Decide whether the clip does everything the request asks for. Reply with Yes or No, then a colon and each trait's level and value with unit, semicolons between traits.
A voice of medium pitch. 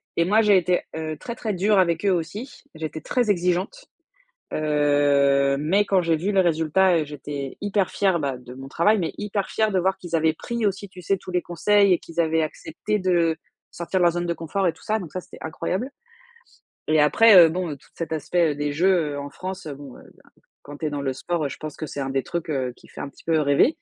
Yes: medium, 170 Hz